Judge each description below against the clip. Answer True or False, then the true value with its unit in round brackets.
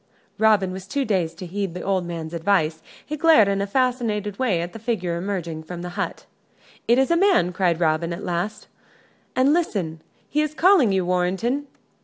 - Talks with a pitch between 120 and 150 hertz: False (195 Hz)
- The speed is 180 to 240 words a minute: True (190 wpm)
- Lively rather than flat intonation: True (5.7 semitones)